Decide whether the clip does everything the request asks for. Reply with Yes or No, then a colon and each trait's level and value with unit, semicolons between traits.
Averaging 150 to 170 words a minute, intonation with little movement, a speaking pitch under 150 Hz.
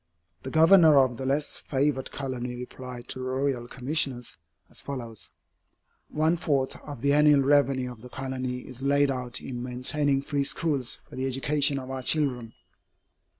Yes: average, 160 wpm; narrow, 2.2 semitones; low, 135 Hz